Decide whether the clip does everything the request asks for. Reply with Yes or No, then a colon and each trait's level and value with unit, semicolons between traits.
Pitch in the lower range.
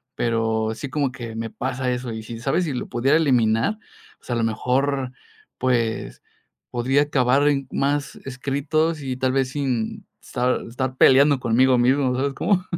Yes: low, 130 Hz